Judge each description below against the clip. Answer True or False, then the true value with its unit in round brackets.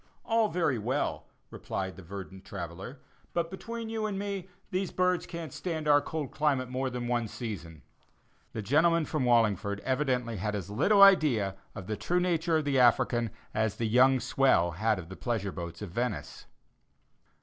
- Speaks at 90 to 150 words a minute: False (170 wpm)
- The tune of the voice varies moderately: False (8.0 semitones)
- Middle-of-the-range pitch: False (125 Hz)